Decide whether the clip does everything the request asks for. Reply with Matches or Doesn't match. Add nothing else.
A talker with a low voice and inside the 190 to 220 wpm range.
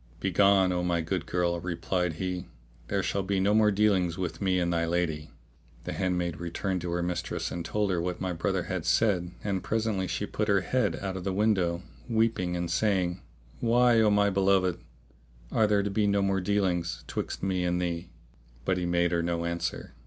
Matches